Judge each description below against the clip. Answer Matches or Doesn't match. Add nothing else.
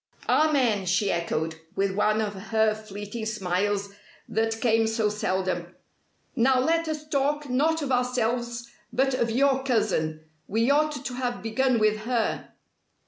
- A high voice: Matches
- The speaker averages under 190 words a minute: Matches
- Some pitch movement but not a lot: Matches